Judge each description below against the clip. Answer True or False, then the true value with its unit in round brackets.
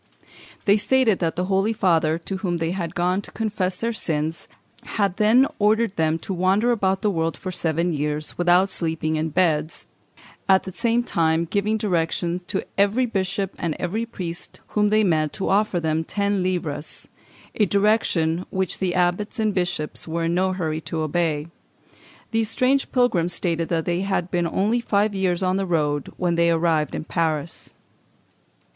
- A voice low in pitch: False (180 Hz)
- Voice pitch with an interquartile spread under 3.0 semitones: False (3.7 semitones)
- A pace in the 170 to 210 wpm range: True (175 wpm)